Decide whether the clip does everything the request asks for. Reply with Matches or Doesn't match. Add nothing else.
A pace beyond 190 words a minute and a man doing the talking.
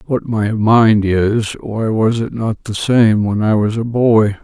Matches